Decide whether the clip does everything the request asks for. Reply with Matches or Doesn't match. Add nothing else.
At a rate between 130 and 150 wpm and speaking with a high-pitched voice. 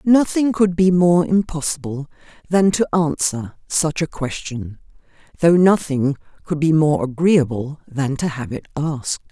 Doesn't match